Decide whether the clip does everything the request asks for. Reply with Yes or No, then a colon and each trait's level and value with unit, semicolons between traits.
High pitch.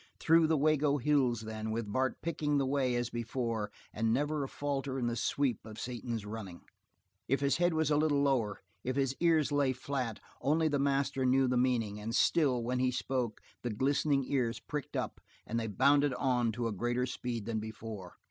No: low, 130 Hz